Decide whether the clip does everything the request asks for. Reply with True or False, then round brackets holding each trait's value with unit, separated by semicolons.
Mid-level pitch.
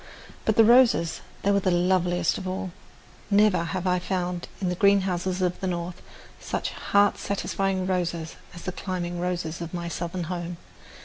True (180 Hz)